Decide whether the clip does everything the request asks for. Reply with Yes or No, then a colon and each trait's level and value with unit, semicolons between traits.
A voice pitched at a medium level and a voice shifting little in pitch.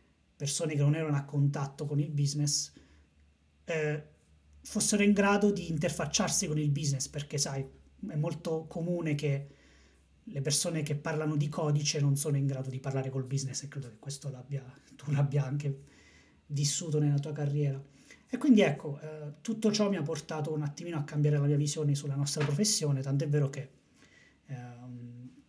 Yes: medium, 145 Hz; narrow, 2.1 semitones